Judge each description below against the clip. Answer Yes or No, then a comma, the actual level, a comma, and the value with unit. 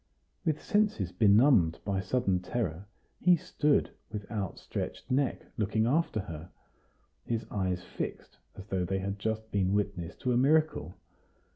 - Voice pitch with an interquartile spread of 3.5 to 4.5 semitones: No, average, 5.1 semitones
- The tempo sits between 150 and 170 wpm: No, average, 140 wpm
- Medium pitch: No, low, 105 Hz